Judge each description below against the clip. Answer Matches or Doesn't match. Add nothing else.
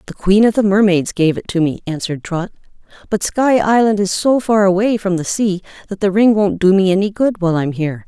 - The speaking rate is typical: Doesn't match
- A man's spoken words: Doesn't match